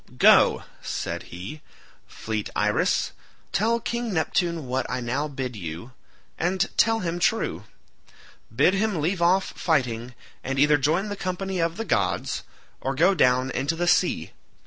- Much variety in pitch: Yes, wide, 6.7 semitones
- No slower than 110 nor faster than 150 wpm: Yes, average, 145 wpm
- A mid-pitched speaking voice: Yes, medium, 160 Hz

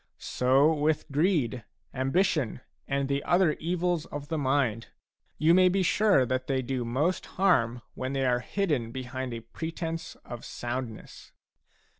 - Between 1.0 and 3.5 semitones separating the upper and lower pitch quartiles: No, average, 4.6 semitones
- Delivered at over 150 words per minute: No, average, 145 wpm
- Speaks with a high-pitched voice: No, medium, 140 Hz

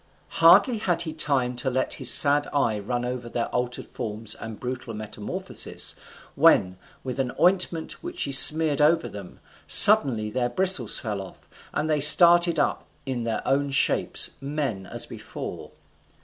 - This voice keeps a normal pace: Yes, average, 155 wpm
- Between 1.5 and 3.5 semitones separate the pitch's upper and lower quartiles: No, average, 5.3 semitones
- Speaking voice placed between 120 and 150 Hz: Yes, low, 135 Hz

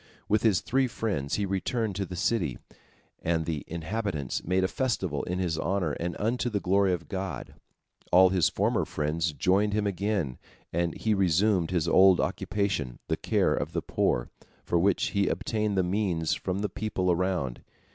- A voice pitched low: Yes, very low, 95 Hz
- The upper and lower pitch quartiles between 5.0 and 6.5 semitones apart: No, average, 3.5 semitones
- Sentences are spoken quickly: No, average, 175 wpm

